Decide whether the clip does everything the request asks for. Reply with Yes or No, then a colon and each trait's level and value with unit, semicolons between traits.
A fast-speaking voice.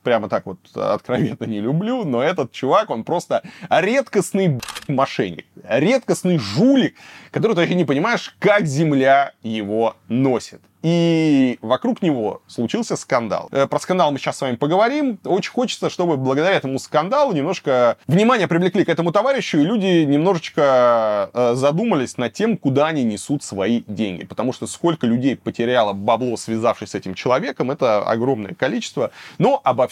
No: average, 150 wpm